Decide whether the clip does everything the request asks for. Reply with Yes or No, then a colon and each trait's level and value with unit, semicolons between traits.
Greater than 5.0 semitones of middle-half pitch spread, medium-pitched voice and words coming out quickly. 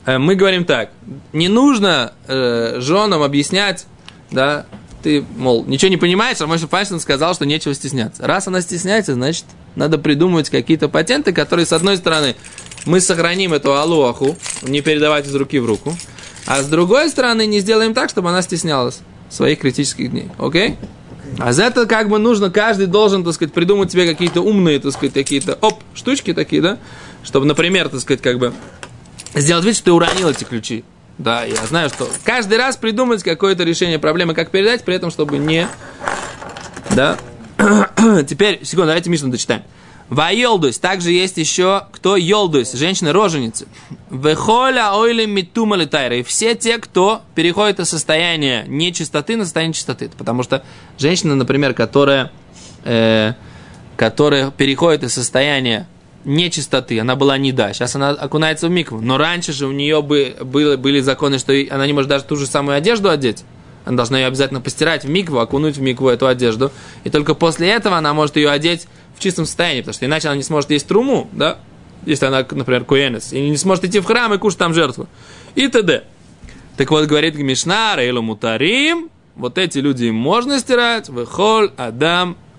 Yes: wide, 5.4 semitones; medium, 155 Hz; fast, 170 wpm